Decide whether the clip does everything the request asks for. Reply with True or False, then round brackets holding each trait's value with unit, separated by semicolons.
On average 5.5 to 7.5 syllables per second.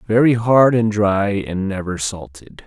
False (3.9 syllables/s)